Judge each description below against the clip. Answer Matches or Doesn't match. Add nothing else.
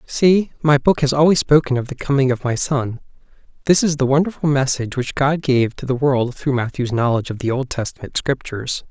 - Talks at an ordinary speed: Doesn't match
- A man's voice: Matches